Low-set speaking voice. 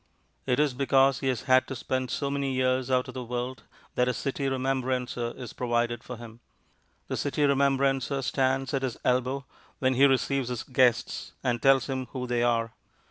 Yes: low, 130 Hz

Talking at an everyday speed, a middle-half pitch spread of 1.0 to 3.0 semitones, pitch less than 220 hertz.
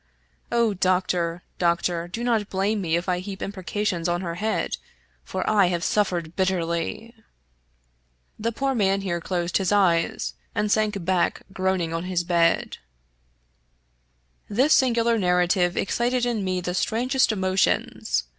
No: average, 145 wpm; average, 3.4 semitones; medium, 185 Hz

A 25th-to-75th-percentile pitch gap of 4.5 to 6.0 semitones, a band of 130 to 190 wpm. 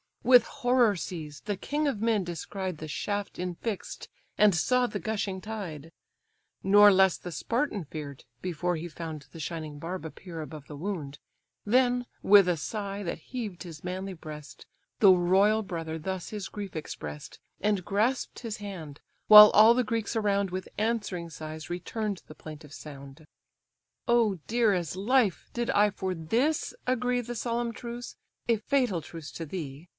Yes: average, 5.2 semitones; average, 160 wpm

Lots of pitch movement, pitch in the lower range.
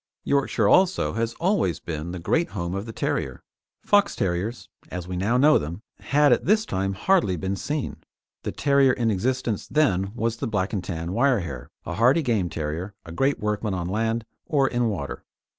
Yes: wide, 6.8 semitones; low, 110 Hz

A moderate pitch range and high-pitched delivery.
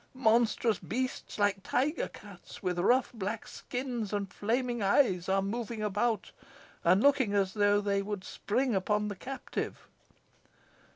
Yes: average, 3.4 semitones; high, 210 Hz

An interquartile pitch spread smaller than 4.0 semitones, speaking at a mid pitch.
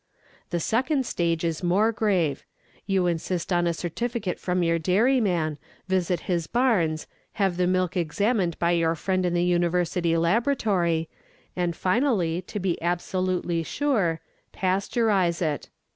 Yes: average, 2.9 semitones; medium, 180 Hz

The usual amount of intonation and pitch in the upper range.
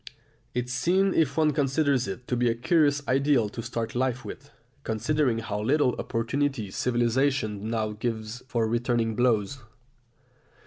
No: average, 3.6 semitones; low, 125 Hz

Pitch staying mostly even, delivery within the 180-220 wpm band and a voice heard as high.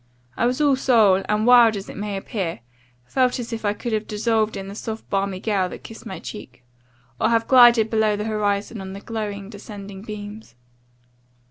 Yes: narrow, 2.3 semitones; average, 195 wpm; high, 210 Hz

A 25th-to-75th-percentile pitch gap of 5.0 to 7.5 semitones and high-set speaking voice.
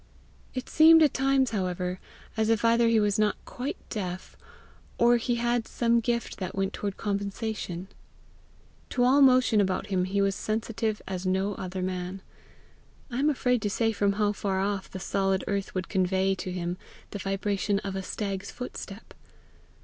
No: average, 3.5 semitones; high, 205 Hz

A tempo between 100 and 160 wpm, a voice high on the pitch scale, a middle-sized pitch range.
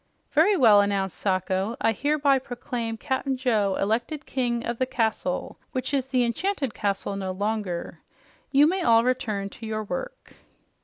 Yes: average, 155 wpm; high, 235 Hz; average, 4.8 semitones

